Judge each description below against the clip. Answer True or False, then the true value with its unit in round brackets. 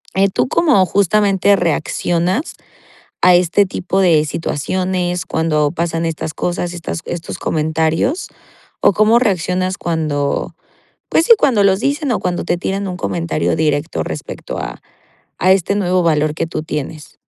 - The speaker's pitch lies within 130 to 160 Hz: False (175 Hz)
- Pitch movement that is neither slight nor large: True (3.3 semitones)